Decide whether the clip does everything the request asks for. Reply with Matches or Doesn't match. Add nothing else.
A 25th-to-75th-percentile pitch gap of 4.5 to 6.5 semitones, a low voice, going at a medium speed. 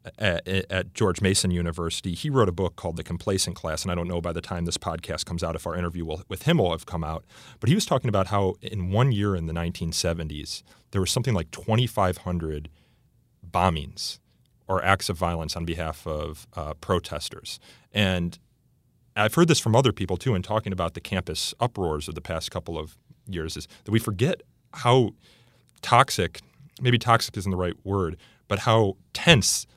Matches